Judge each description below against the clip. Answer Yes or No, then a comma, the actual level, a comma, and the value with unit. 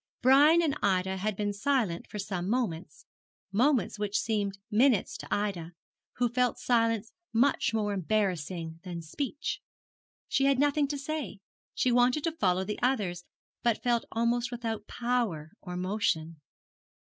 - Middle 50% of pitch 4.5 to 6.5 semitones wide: Yes, average, 4.9 semitones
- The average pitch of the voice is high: Yes, high, 220 Hz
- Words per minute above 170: No, average, 145 wpm